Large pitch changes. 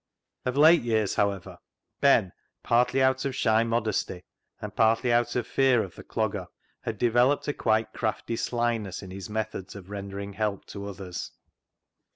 No: average, 3.3 semitones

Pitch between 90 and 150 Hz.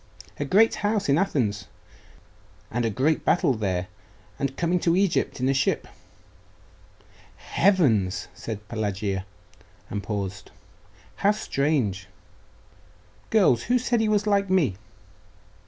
Yes: low, 135 Hz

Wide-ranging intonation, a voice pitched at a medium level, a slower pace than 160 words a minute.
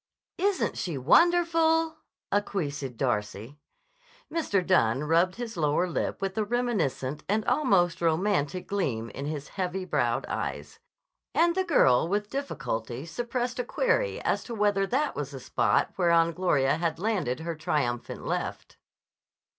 Yes: wide, 8.6 semitones; medium, 180 Hz; average, 140 wpm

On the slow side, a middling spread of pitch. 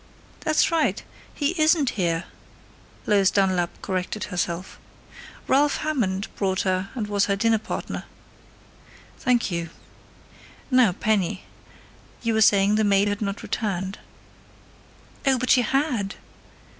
Yes: slow, 120 wpm; average, 4.6 semitones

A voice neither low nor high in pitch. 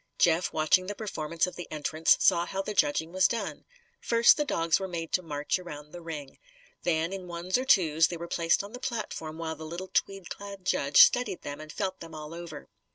Yes: medium, 170 Hz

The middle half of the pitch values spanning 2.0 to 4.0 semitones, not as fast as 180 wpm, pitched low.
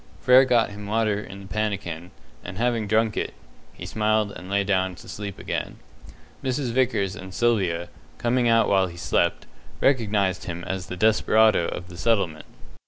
Yes: average, 3.4 semitones; average, 170 wpm; low, 105 Hz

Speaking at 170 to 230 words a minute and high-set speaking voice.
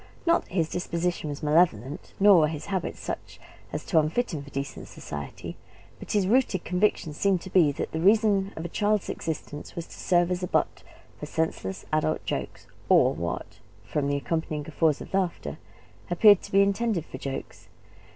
No: average, 185 wpm; medium, 170 Hz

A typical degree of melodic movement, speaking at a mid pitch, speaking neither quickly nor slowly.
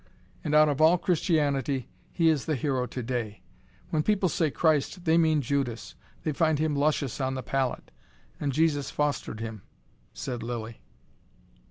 Yes: average, 3.9 semitones; medium, 145 Hz; average, 160 wpm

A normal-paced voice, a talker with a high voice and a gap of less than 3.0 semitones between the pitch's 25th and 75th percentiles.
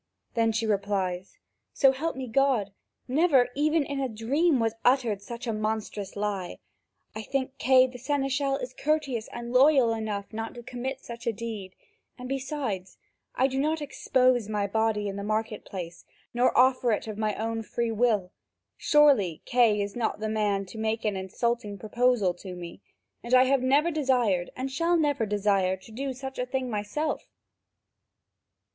No: average, 170 wpm; high, 235 Hz; average, 4.1 semitones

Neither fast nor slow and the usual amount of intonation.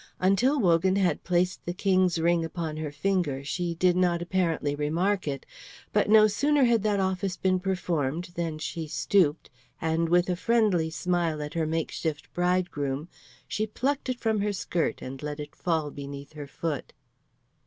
Yes: average, 165 wpm; average, 3.5 semitones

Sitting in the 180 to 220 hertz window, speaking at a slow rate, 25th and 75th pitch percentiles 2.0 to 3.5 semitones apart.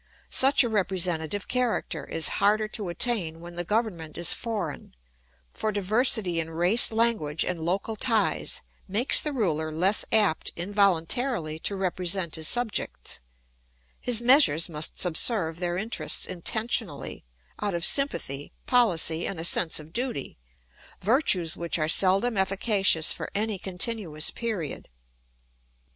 No: high, 190 Hz; slow, 130 wpm; average, 5.3 semitones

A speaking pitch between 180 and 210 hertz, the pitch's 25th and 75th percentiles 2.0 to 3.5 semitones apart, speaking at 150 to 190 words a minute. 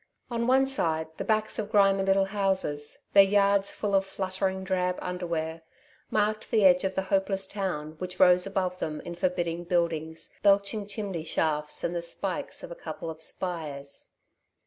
Yes: high, 190 Hz; average, 2.9 semitones; average, 170 wpm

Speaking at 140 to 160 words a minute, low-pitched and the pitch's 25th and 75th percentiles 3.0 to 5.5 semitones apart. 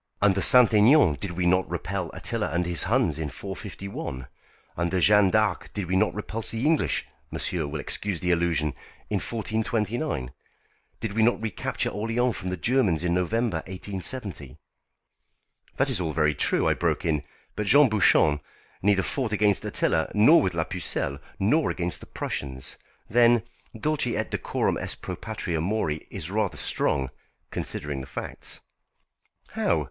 Yes: average, 155 wpm; very low, 95 Hz; average, 4.9 semitones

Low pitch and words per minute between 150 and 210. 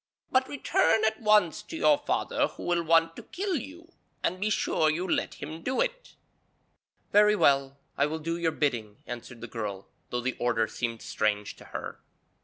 No: medium, 165 Hz; average, 185 wpm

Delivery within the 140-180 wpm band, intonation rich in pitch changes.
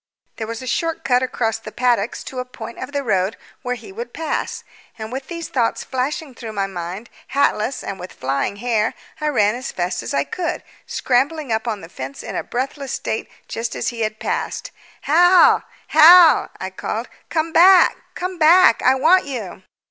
No: average, 190 wpm; wide, 6.0 semitones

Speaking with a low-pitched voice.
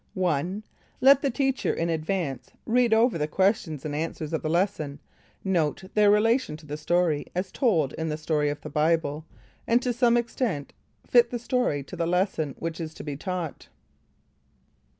No: medium, 170 Hz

